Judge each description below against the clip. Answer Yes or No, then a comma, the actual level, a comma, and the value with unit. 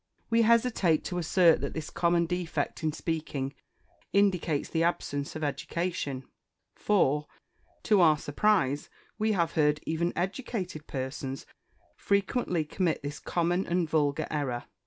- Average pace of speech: No, slow, 130 wpm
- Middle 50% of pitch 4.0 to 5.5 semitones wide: No, average, 3.6 semitones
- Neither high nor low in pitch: Yes, medium, 165 Hz